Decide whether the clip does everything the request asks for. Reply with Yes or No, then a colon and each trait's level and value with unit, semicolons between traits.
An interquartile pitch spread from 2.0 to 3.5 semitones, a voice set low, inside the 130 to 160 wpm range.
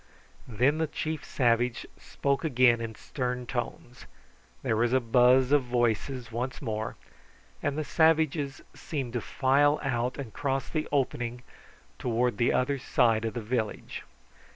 Yes: average, 2.8 semitones; low, 125 Hz; average, 145 wpm